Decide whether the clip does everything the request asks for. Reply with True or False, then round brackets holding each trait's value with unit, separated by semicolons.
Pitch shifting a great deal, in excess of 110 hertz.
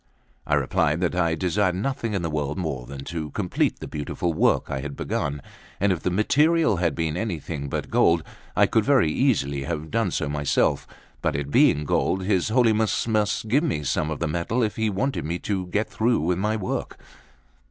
False (6.0 semitones; 90 Hz)